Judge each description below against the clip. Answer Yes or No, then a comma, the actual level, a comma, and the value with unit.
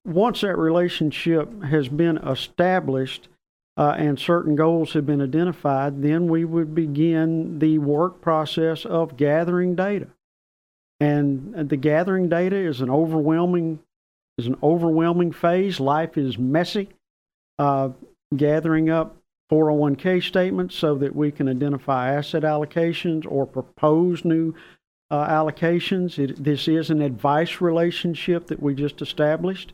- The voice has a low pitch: No, medium, 160 Hz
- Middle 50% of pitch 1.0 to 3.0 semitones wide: Yes, narrow, 2.6 semitones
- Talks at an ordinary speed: No, slow, 130 wpm